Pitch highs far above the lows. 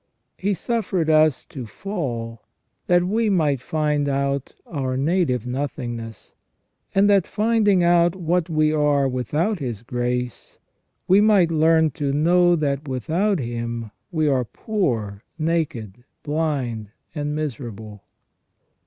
Yes: wide, 5.8 semitones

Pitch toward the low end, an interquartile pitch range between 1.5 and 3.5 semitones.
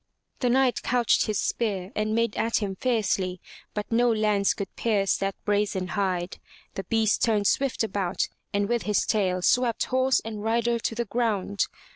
No: high, 215 Hz; average, 2.9 semitones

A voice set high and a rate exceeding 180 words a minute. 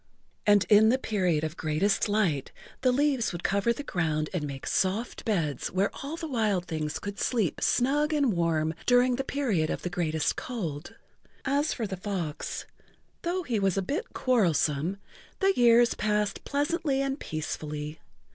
No: high, 205 Hz; average, 160 wpm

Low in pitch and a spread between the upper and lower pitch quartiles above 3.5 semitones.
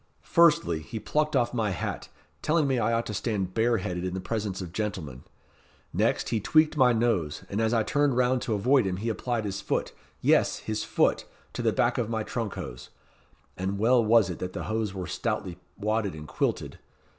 Yes: low, 110 Hz; average, 4.2 semitones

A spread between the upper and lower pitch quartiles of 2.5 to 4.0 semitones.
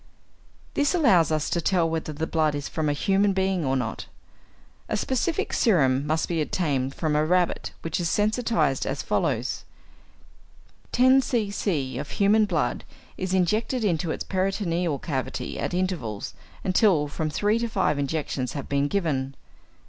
No: wide, 5.4 semitones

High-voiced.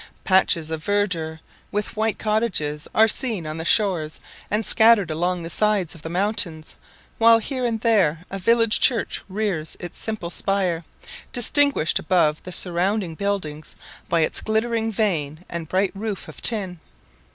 Yes: high, 195 Hz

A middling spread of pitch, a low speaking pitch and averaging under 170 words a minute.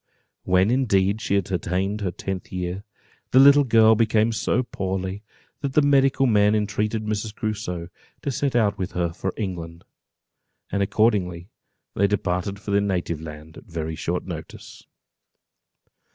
Yes: average, 3.3 semitones; low, 100 Hz; average, 150 wpm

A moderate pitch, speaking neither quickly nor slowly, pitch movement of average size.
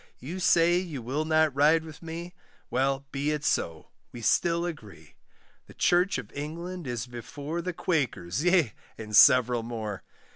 No: medium, 145 Hz; average, 155 wpm; wide, 5.7 semitones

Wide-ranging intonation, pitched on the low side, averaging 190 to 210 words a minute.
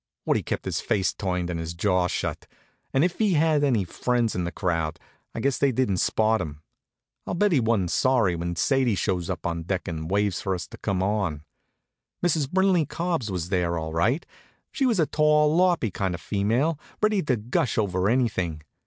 Yes: wide, 8.4 semitones; low, 105 Hz; average, 195 wpm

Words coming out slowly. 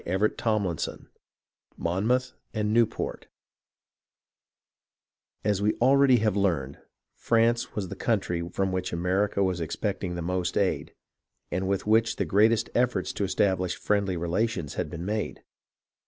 Yes: slow, 130 wpm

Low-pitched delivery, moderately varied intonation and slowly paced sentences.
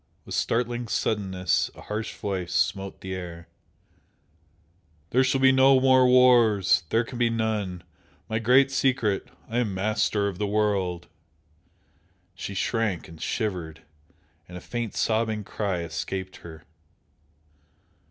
Yes: low, 105 Hz; average, 4.3 semitones; slow, 130 wpm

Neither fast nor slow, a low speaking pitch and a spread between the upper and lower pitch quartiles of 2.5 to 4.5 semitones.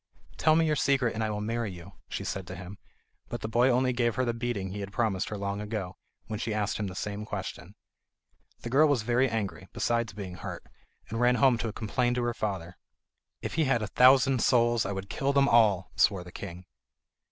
No: fast, 220 wpm; low, 110 Hz; average, 3.6 semitones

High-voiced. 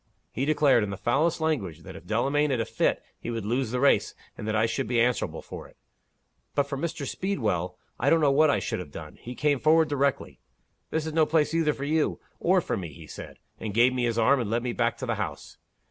No: low, 130 Hz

